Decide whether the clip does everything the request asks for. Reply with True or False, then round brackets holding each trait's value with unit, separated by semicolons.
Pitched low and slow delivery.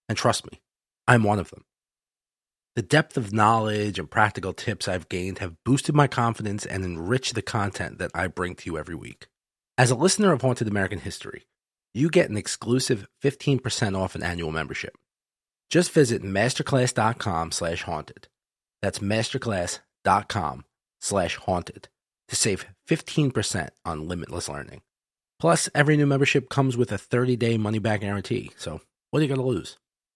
False (110 Hz; 150 wpm)